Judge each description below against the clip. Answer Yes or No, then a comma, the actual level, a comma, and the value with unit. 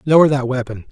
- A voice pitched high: No, low, 135 Hz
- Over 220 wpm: No, average, 200 wpm